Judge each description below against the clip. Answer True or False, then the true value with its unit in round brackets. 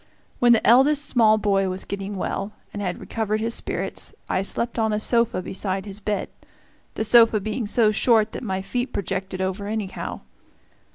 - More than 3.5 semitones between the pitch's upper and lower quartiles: False (2.7 semitones)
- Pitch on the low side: False (210 Hz)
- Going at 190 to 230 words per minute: False (175 wpm)